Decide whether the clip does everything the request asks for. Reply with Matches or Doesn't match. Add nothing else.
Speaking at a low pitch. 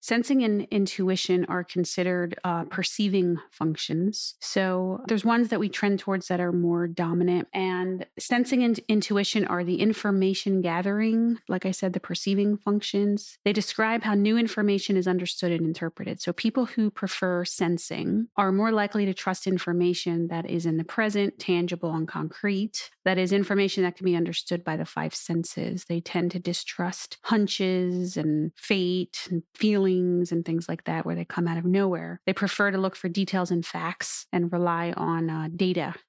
Doesn't match